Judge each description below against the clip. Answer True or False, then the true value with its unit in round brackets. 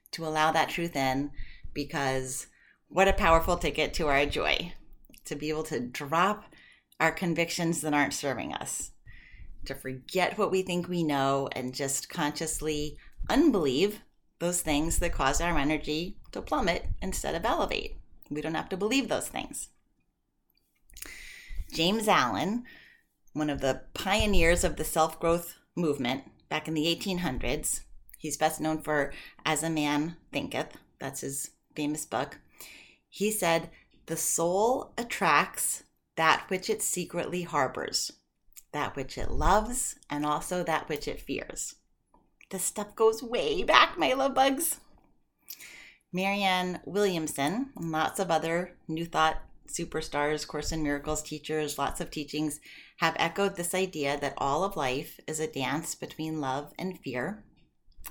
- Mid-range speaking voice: True (160 Hz)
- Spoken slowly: False (145 wpm)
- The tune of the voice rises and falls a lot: False (3.5 semitones)